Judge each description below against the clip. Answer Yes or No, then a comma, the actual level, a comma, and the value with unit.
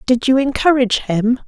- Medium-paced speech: Yes, average, 165 wpm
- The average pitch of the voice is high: Yes, very high, 250 Hz